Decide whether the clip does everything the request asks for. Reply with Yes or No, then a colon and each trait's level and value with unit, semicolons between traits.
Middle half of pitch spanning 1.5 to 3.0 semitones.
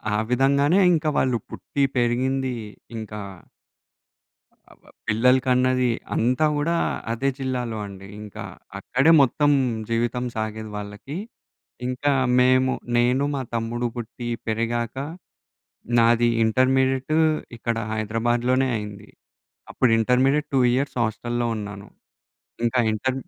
Yes: narrow, 2.6 semitones